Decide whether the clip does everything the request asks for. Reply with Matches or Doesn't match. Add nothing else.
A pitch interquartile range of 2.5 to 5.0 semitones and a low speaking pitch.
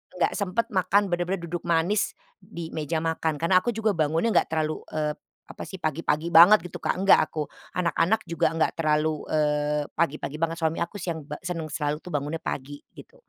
Doesn't match